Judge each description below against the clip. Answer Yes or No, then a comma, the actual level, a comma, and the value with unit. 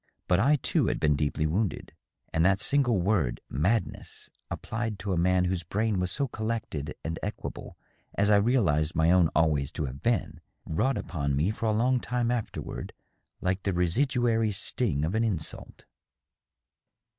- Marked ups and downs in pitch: Yes, wide, 5.8 semitones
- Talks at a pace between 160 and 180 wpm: Yes, average, 170 wpm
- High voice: No, very low, 95 Hz